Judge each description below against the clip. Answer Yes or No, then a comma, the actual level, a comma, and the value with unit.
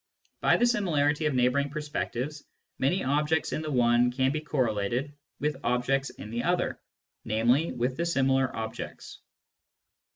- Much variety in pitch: No, average, 3.5 semitones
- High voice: No, low, 135 Hz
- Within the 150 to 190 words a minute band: No, average, 140 wpm